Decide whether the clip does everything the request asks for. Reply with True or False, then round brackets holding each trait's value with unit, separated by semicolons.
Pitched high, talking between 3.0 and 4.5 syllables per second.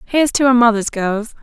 False (235 Hz; 5.6 syllables/s)